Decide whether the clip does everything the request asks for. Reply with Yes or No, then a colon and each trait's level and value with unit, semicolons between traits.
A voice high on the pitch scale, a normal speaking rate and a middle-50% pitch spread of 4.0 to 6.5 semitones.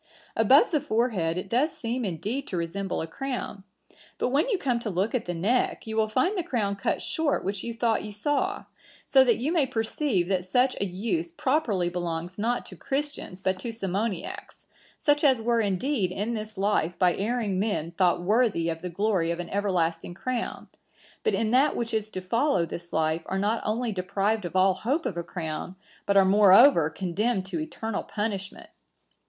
Yes: high, 210 Hz; average, 195 wpm; average, 5.1 semitones